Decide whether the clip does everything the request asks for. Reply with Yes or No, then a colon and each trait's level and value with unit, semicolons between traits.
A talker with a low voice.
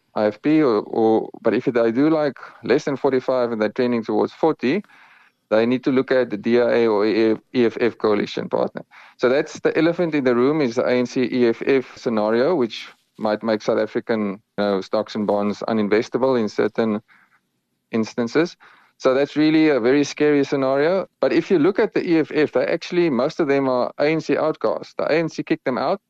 Yes: low, 125 Hz